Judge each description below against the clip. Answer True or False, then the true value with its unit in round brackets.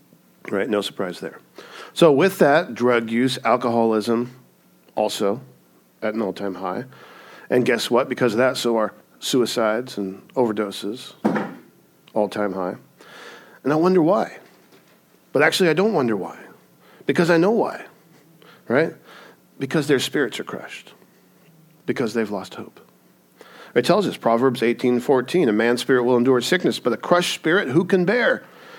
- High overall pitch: False (120 Hz)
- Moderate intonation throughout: True (4.0 semitones)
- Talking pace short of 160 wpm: True (145 wpm)